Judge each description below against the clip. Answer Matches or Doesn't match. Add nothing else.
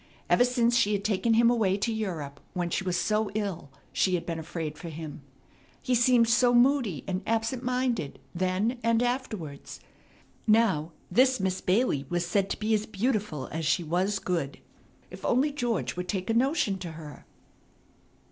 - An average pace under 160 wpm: Doesn't match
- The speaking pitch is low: Doesn't match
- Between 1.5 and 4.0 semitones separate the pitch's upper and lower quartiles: Doesn't match